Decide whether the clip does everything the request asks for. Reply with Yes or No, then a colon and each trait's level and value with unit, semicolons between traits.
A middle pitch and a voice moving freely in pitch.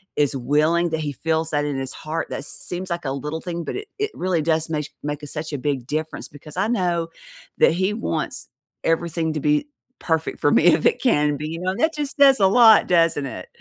No: medium, 160 Hz; average, 3.5 semitones